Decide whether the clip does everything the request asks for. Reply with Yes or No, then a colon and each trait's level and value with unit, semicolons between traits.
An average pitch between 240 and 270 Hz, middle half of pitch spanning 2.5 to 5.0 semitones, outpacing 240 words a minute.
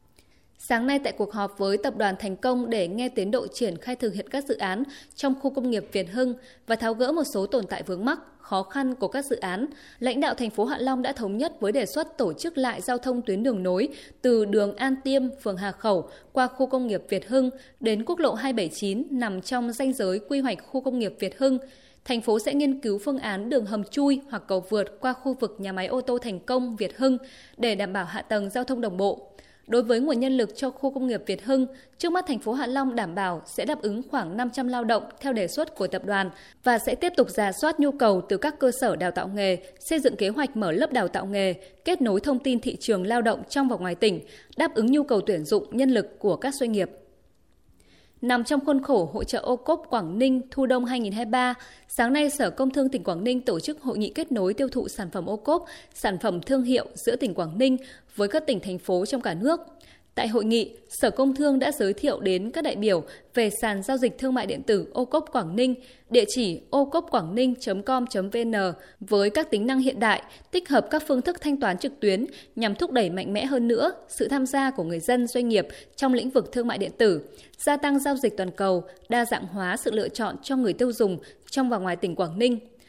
Yes: high, 245 Hz; average, 4.7 semitones; fast, 250 wpm